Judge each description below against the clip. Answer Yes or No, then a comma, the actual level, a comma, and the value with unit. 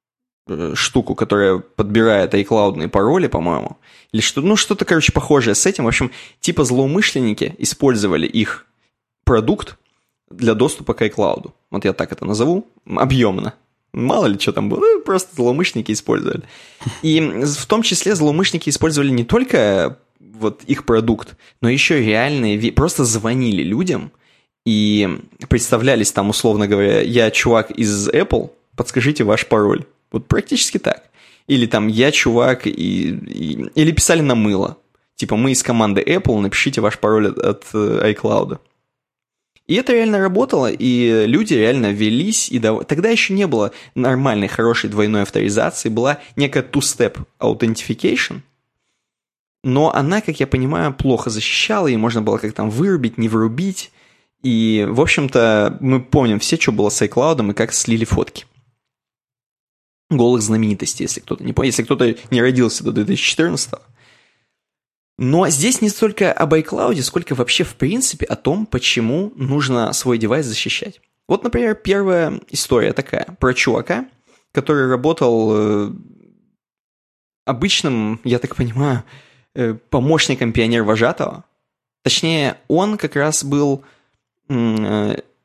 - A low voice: Yes, low, 125 Hz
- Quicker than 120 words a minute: Yes, average, 135 wpm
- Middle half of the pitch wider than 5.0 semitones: Yes, wide, 5.4 semitones